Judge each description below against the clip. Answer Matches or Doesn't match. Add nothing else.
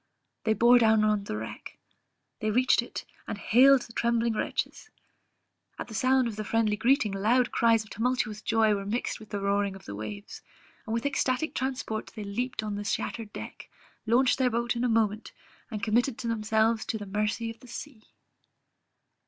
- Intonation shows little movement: Matches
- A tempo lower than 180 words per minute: Doesn't match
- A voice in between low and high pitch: Doesn't match